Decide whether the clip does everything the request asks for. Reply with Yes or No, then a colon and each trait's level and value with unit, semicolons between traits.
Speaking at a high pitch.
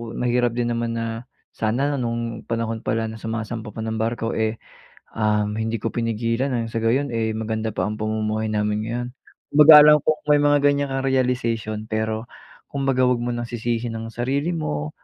No: low, 115 Hz